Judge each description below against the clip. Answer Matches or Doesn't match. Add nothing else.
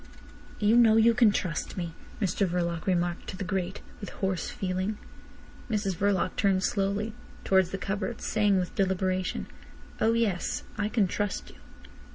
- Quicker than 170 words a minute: Doesn't match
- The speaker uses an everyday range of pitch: Doesn't match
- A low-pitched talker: Doesn't match